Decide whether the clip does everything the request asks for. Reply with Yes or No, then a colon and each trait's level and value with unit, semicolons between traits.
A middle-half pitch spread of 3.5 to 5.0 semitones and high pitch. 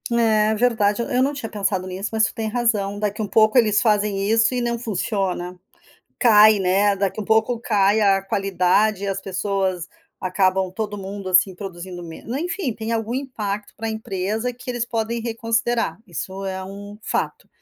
No: average, 2.7 semitones; high, 210 Hz